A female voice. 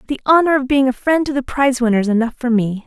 Yes: female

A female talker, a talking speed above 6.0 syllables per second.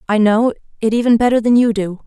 Yes: female; 6.3 syllables/s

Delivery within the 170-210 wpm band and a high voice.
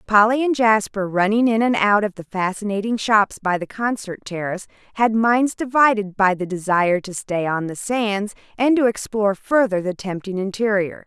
Yes: average, 180 wpm; high, 210 Hz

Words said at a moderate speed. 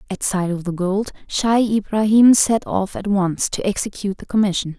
Yes: average, 190 wpm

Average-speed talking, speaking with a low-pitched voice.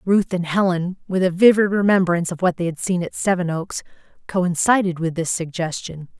No: average, 185 wpm; medium, 180 Hz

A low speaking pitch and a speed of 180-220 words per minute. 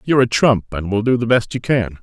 No: low, 115 Hz; fast, 295 wpm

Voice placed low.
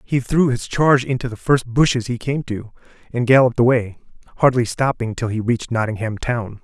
Yes: low, 120 Hz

